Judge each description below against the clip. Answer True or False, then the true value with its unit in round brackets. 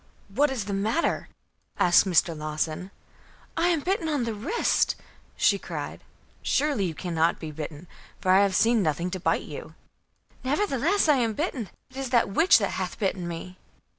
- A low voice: False (200 Hz)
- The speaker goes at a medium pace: True (170 wpm)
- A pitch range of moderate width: False (7.9 semitones)